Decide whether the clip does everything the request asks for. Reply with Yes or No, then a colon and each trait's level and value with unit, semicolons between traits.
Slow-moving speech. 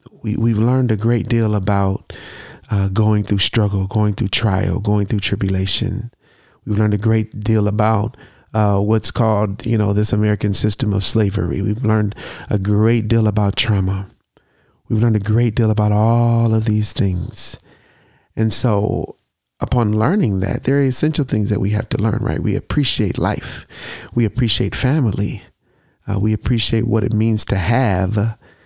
No: average, 165 wpm